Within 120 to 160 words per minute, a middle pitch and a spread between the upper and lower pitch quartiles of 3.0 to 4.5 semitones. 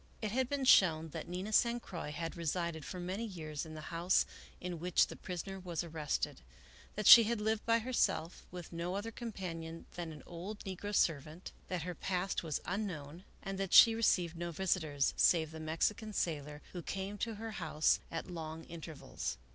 No: average, 185 wpm; medium, 175 Hz; average, 3.9 semitones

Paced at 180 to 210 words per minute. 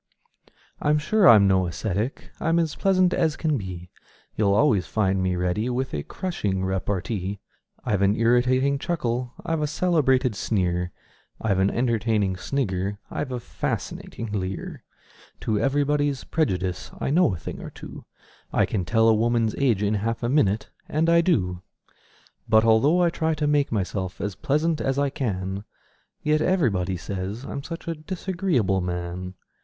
No: average, 160 wpm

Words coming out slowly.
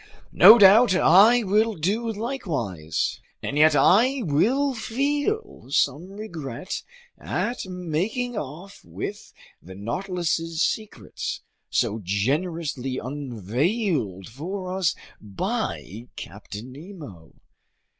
Yes: slow, 95 wpm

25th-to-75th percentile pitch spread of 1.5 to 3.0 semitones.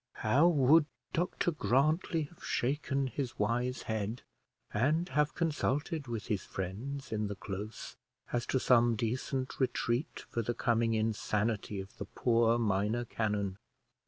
No: average, 4.5 semitones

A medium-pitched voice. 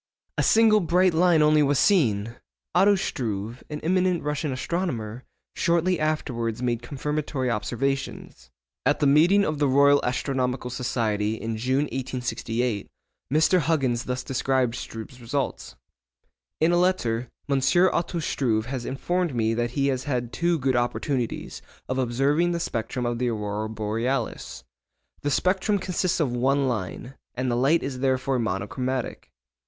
No: low, 130 Hz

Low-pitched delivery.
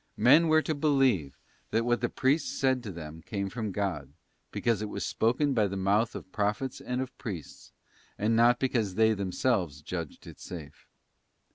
Yes: low, 110 Hz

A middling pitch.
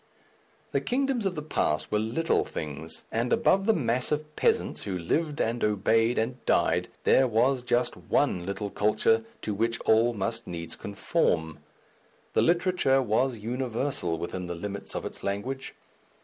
No: low, 115 Hz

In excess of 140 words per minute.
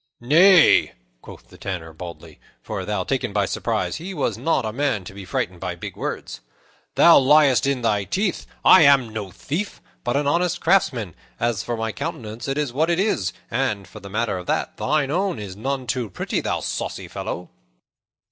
Yes: average, 190 wpm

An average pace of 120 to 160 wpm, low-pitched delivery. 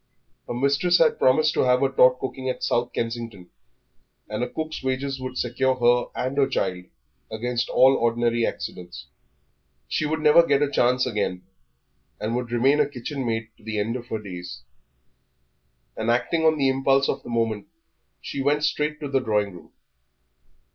No: average, 175 wpm; low, 125 Hz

